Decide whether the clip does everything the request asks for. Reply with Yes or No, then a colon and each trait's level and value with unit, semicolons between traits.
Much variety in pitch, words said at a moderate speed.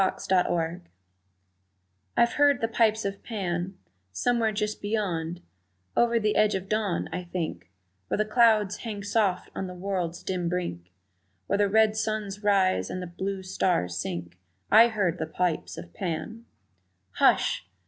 No: average, 3.6 semitones; average, 150 wpm